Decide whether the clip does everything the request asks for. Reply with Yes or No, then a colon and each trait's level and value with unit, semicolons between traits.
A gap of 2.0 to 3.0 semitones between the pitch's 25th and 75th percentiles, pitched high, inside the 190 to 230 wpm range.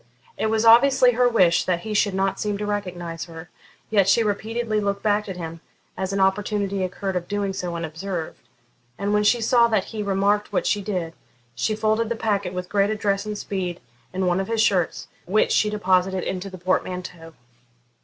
Yes: narrow, 2.6 semitones; high, 200 Hz; average, 195 wpm